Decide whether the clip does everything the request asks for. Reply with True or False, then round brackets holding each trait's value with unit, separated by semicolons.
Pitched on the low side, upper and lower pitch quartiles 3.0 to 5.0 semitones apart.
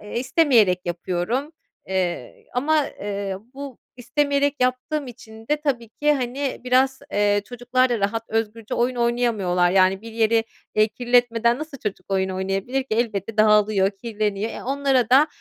False (230 Hz; 4.0 semitones)